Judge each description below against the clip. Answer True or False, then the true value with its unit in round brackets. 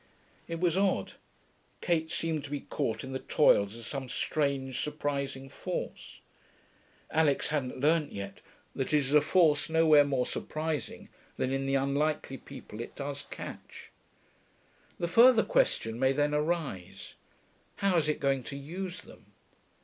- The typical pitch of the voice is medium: True (145 Hz)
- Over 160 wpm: False (150 wpm)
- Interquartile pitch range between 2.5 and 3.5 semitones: True (3.1 semitones)